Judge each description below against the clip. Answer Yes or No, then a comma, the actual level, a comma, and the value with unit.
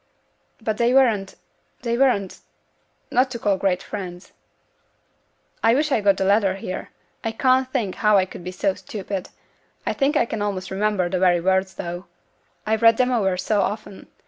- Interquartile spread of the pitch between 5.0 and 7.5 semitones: No, average, 3.7 semitones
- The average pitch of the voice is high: Yes, high, 205 Hz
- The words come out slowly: No, average, 175 wpm